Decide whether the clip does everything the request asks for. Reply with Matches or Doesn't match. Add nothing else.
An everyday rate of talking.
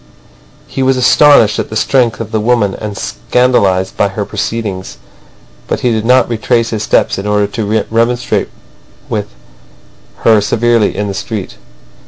Matches